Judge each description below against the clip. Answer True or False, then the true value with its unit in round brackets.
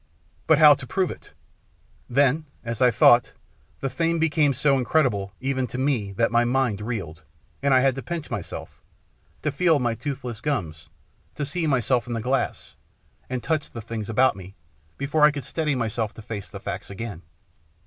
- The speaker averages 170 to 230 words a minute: True (180 wpm)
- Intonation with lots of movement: False (4.1 semitones)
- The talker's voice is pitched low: True (130 Hz)